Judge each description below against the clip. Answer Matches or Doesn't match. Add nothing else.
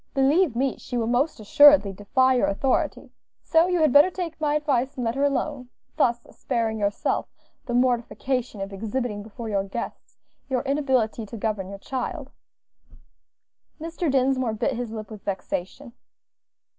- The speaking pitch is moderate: Doesn't match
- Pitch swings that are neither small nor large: Matches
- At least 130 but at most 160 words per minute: Matches